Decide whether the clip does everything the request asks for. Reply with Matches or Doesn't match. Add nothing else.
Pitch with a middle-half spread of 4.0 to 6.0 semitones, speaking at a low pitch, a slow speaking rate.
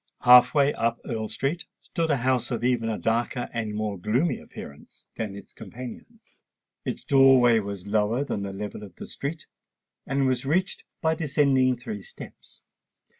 Doesn't match